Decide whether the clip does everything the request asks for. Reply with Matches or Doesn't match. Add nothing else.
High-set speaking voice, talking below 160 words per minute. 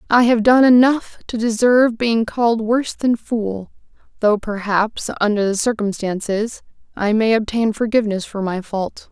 Matches